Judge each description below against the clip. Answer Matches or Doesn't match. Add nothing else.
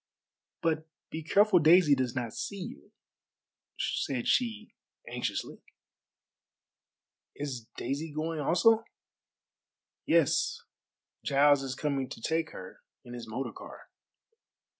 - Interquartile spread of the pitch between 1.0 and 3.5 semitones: Doesn't match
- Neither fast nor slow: Doesn't match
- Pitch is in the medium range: Matches